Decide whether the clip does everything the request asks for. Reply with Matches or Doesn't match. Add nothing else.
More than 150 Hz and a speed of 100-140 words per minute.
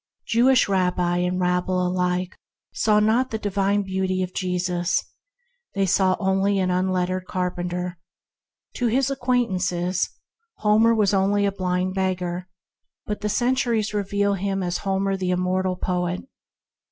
Matches